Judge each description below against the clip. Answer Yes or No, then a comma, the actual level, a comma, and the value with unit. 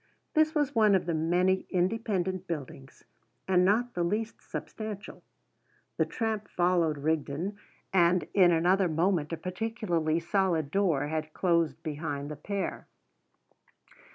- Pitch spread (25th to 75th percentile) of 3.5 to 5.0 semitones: Yes, average, 3.8 semitones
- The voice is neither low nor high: Yes, medium, 180 Hz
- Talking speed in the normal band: No, slow, 125 wpm